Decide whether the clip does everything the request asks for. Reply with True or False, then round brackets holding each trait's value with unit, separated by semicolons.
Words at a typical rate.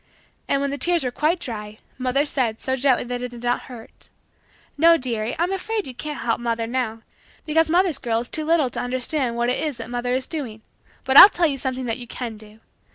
False (225 wpm)